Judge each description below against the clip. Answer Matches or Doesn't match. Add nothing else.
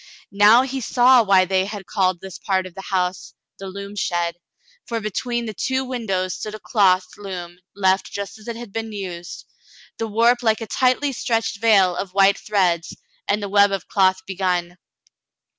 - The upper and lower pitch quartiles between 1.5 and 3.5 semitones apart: Matches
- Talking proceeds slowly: Doesn't match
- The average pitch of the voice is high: Matches